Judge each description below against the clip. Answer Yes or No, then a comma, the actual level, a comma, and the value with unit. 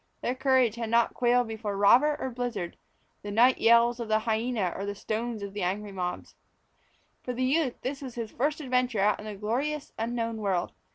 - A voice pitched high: Yes, high, 235 Hz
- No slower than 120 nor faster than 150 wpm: No, average, 190 wpm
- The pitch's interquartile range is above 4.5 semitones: No, average, 3.2 semitones